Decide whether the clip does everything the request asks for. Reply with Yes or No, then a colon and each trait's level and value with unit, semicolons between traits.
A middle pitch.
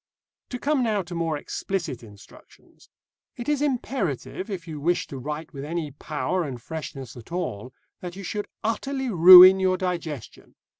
Yes: medium, 175 Hz